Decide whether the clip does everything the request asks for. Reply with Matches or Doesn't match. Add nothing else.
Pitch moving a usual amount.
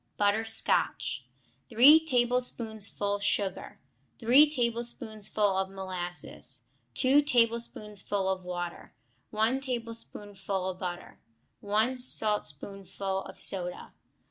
Matches